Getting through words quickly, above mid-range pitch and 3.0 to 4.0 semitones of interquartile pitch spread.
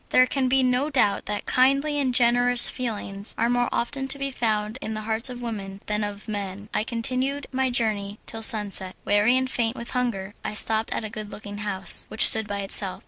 Yes: fast, 210 wpm; high, 225 Hz; average, 3.5 semitones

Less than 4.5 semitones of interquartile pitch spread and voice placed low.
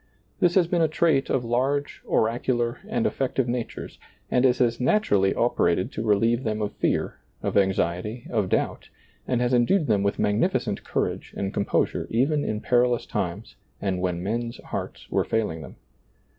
Yes: average, 4.1 semitones; low, 120 Hz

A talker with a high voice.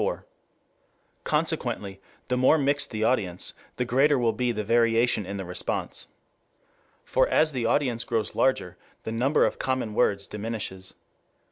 No: low, 115 Hz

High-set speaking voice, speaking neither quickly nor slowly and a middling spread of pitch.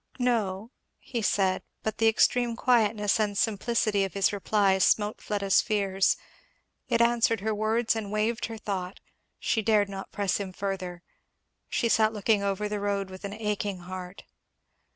No: high, 205 Hz; average, 155 wpm; narrow, 2.3 semitones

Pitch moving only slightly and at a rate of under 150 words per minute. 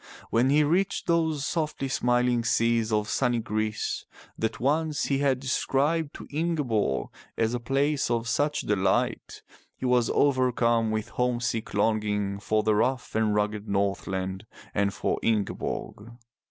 No: average, 4.2 semitones; average, 140 wpm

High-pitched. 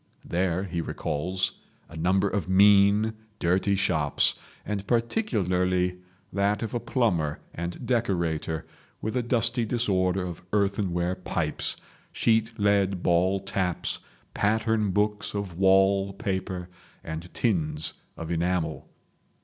No: very low, 95 Hz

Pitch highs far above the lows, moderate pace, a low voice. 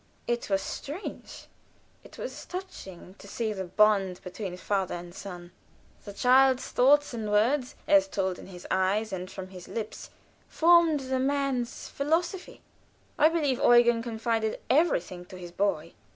No: wide, 6.5 semitones; average, 150 wpm; high, 225 Hz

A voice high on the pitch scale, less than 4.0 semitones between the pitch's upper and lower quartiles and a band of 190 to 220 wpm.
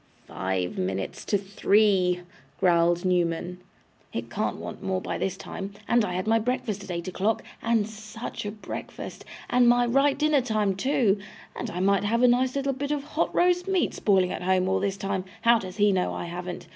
No: high, 200 Hz; average, 4.6 semitones; average, 195 wpm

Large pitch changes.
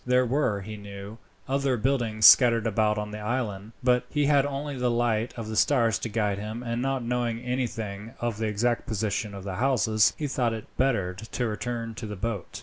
No: average, 2.8 semitones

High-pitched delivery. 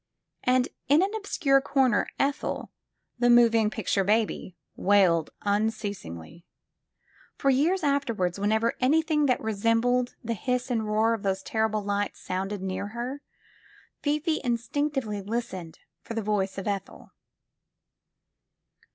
Yes: high, 225 Hz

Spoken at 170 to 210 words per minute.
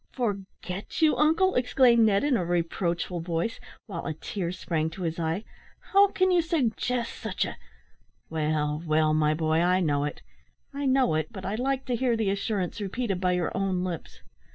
Yes: average, 185 wpm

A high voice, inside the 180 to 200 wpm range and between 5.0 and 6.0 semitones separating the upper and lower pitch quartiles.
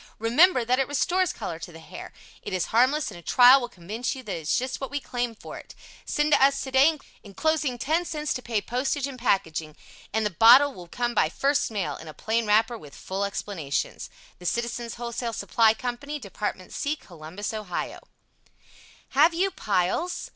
Yes: high, 235 Hz; average, 190 wpm; wide, 5.5 semitones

